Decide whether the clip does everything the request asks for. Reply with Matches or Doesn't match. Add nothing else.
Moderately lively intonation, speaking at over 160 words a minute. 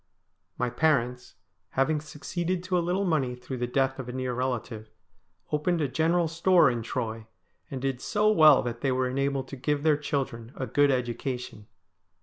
Matches